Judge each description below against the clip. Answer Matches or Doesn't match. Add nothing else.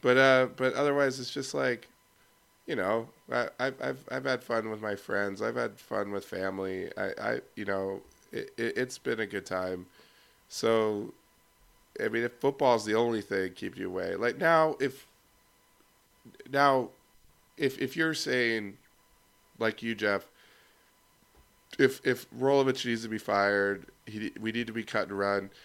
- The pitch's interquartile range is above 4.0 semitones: Matches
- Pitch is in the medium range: Doesn't match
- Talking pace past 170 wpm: Doesn't match